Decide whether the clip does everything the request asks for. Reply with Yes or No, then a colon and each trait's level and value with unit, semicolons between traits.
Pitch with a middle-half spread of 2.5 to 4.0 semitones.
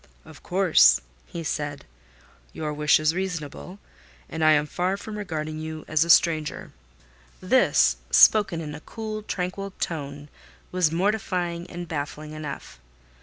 Yes: average, 3.2 semitones